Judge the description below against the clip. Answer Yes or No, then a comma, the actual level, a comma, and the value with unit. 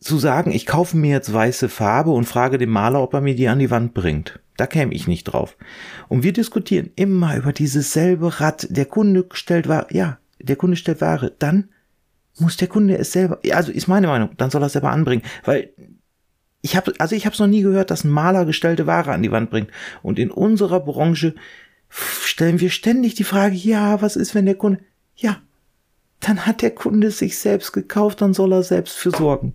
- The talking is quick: Yes, fast, 220 wpm